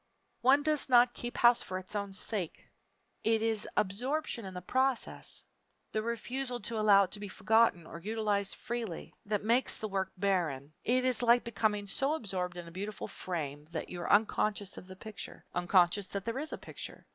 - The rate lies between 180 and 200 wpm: Yes, average, 190 wpm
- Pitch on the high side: Yes, high, 210 Hz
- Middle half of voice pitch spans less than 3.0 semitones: No, average, 4.1 semitones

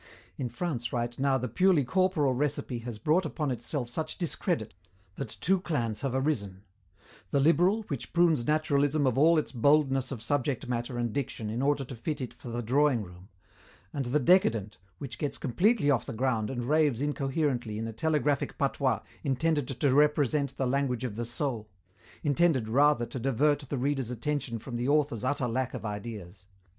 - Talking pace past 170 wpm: Yes, average, 180 wpm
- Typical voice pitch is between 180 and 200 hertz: No, low, 135 Hz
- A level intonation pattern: No, average, 3.9 semitones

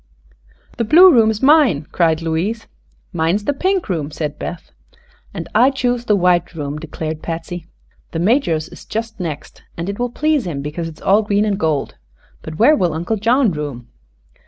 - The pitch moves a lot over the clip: Yes, wide, 6.4 semitones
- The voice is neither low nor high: Yes, medium, 180 Hz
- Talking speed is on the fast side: No, average, 185 wpm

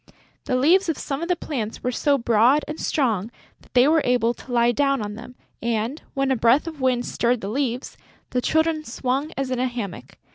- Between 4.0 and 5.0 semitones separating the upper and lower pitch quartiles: No, average, 3.5 semitones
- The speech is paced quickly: Yes, fast, 215 wpm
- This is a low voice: No, very high, 255 Hz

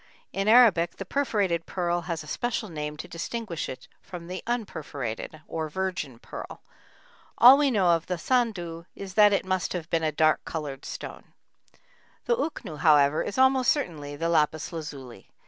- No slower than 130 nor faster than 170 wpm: Yes, average, 165 wpm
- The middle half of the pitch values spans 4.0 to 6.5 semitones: Yes, average, 4.9 semitones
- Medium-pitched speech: Yes, medium, 170 Hz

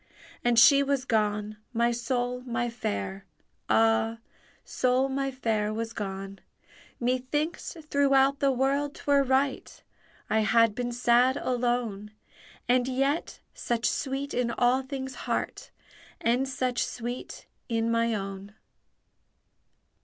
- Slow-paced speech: Yes, slow, 115 wpm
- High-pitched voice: Yes, high, 245 Hz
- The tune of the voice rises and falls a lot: No, average, 2.9 semitones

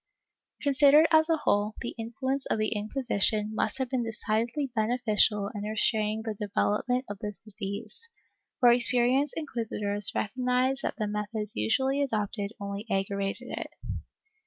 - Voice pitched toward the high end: Yes, high, 220 Hz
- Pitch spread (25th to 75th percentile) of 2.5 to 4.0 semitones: Yes, average, 3.5 semitones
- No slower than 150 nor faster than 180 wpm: No, average, 140 wpm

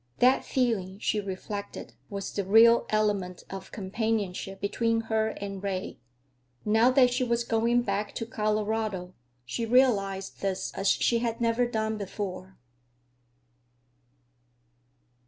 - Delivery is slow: Yes, slow, 120 wpm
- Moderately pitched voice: No, high, 215 Hz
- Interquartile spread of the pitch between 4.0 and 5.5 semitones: No, average, 2.8 semitones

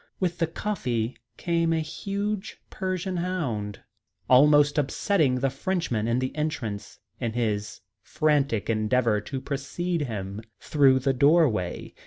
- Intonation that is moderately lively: No, wide, 6.5 semitones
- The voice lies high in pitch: No, medium, 140 Hz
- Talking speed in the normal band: No, slow, 125 wpm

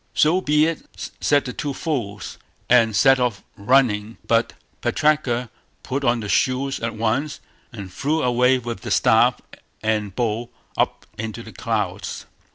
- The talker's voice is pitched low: Yes, low, 120 Hz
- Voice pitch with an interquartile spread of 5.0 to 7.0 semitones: No, average, 3.9 semitones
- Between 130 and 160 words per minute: Yes, average, 150 wpm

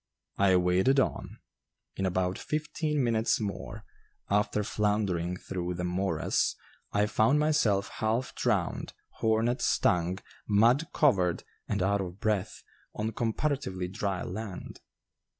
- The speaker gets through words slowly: Yes, slow, 115 wpm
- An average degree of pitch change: Yes, average, 3.8 semitones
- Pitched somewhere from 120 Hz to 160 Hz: No, low, 105 Hz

